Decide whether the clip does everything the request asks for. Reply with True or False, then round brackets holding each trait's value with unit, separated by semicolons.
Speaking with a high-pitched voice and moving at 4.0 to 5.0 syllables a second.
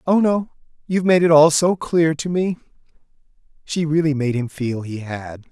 False (155 Hz; 4.9 syllables/s)